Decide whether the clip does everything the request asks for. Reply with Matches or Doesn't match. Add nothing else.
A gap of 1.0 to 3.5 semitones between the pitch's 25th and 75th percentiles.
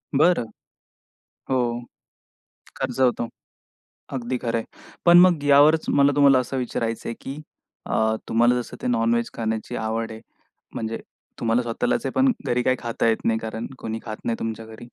Matches